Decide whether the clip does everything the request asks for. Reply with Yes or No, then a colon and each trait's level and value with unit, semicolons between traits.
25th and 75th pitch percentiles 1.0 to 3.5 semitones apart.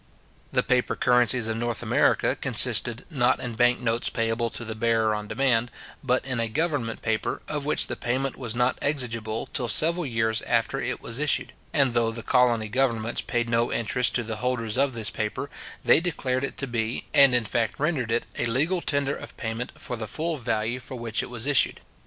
Yes: average, 2.8 semitones